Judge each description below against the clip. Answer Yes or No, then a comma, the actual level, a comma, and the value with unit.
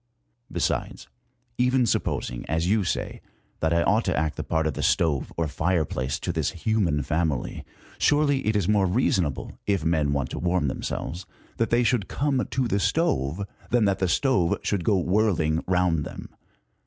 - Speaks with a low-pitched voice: Yes, very low, 90 Hz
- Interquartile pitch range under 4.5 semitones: No, wide, 5.4 semitones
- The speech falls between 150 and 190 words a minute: Yes, average, 175 wpm